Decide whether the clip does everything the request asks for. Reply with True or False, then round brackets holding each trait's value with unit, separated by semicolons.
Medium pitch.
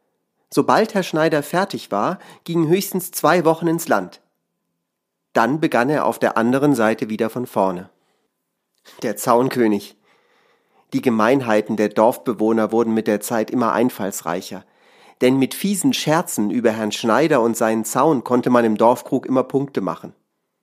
False (125 Hz)